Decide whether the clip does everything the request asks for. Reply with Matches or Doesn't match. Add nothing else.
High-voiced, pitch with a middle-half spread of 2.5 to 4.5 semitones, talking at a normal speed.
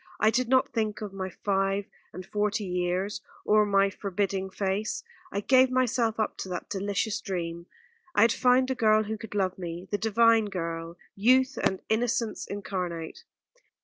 Matches